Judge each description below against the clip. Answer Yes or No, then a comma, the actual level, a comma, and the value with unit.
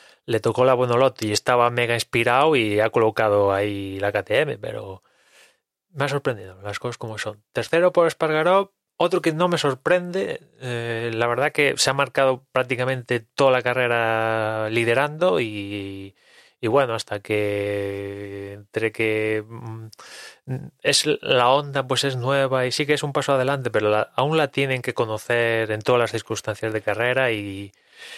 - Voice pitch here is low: Yes, low, 120 Hz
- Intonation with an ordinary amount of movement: Yes, average, 4.1 semitones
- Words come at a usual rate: Yes, average, 160 wpm